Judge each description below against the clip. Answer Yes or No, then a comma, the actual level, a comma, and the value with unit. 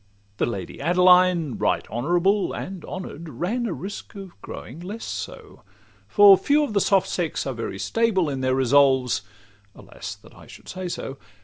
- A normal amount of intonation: No, wide, 6.7 semitones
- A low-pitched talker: No, medium, 175 Hz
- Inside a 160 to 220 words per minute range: Yes, average, 165 wpm